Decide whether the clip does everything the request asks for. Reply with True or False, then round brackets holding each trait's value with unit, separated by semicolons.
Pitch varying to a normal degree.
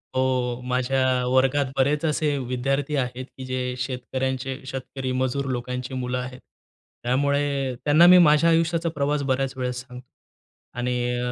False (2.0 semitones)